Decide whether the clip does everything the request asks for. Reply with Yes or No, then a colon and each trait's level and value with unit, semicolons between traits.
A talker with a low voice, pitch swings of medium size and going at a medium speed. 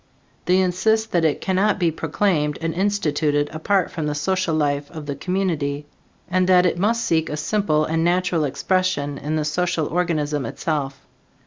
No: medium, 165 Hz; average, 3.7 semitones; average, 170 wpm